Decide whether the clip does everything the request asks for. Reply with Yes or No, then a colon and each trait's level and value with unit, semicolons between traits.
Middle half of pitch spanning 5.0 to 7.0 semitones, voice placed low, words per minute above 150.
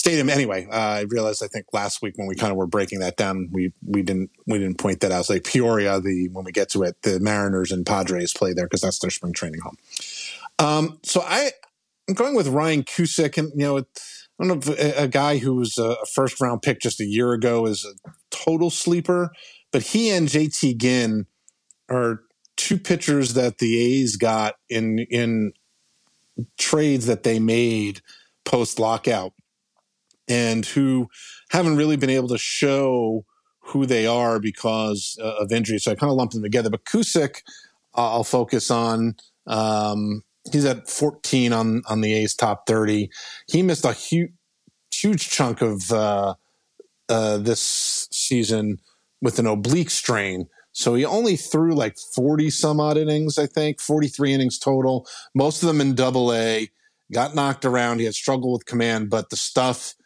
Yes: wide, 5.4 semitones; low, 120 Hz; average, 180 wpm